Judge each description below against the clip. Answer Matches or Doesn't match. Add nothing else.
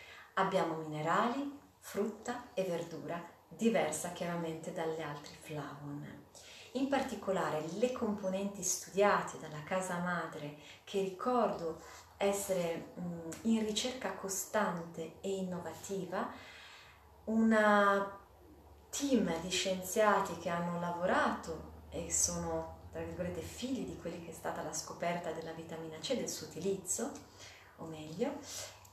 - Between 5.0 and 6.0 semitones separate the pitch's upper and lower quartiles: Doesn't match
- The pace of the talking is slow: Matches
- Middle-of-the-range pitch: Matches